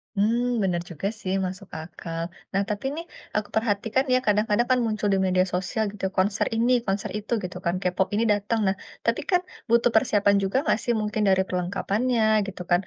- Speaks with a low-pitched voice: No, high, 205 Hz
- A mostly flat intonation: No, average, 3.1 semitones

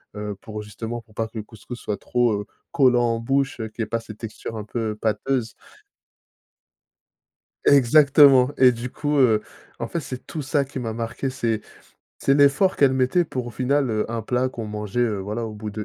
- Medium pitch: No, low, 120 Hz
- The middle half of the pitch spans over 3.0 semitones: Yes, average, 3.4 semitones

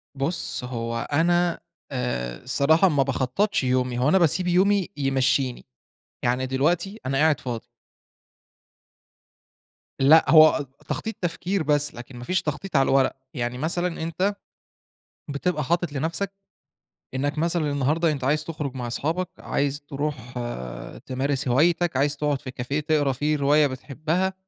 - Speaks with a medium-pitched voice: Yes, medium, 145 Hz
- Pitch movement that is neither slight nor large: Yes, average, 4.1 semitones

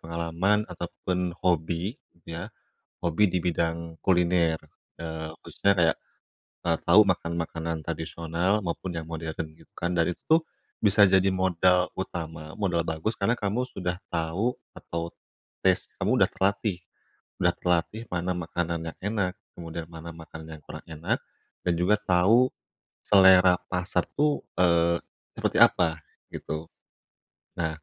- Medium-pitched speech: No, very low, 85 Hz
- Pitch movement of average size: No, narrow, 2.3 semitones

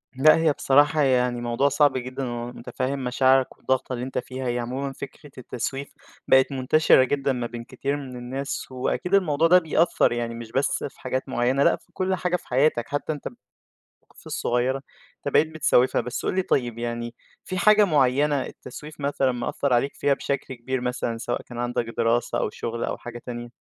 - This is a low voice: Yes, low, 130 Hz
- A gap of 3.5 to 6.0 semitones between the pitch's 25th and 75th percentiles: No, average, 2.7 semitones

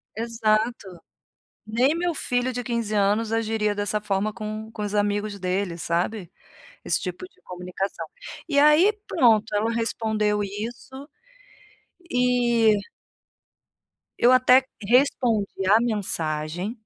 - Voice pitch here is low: No, high, 215 Hz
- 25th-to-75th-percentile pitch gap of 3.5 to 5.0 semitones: No, average, 3.0 semitones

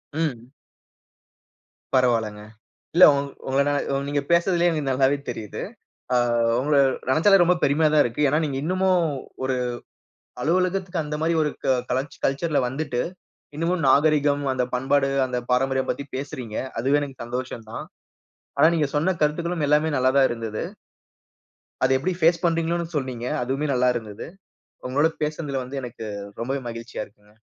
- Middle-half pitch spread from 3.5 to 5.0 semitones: Yes, average, 3.9 semitones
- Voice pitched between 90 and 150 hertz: Yes, medium, 140 Hz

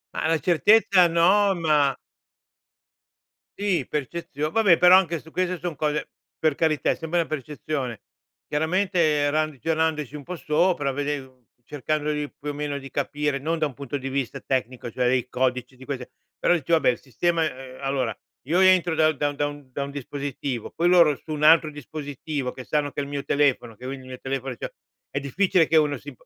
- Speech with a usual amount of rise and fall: Yes, average, 3.1 semitones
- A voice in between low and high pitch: Yes, medium, 150 Hz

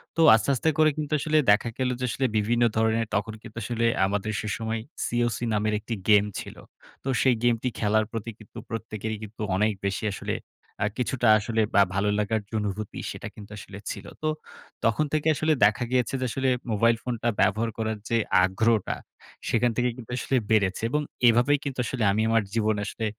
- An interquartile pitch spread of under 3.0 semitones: Yes, narrow, 2.4 semitones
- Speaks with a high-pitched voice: No, low, 115 Hz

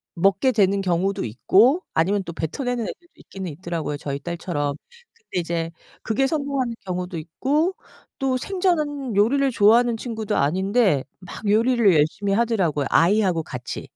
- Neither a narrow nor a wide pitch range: No, wide, 6.5 semitones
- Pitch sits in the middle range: No, high, 200 Hz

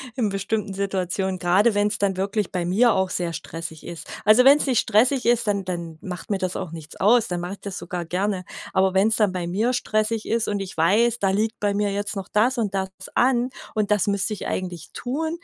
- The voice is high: Yes, high, 200 Hz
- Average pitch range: Yes, average, 3.1 semitones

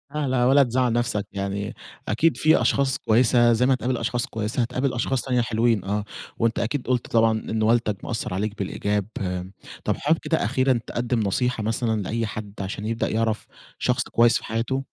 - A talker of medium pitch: No, low, 115 Hz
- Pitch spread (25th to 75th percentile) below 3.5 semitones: Yes, average, 2.8 semitones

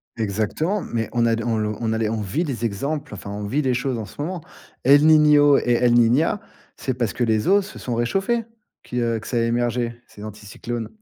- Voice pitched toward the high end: No, low, 120 Hz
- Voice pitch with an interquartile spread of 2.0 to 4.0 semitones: No, average, 4.5 semitones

